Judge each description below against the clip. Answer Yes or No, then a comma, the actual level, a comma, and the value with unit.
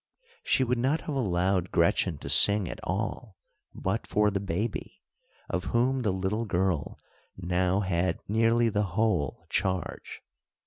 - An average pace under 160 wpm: Yes, average, 140 wpm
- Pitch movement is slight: No, average, 3.9 semitones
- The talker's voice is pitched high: No, very low, 95 Hz